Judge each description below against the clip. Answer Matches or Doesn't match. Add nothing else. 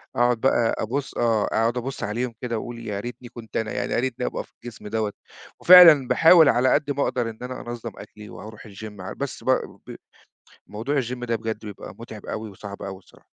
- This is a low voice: Matches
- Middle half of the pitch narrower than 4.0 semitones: Matches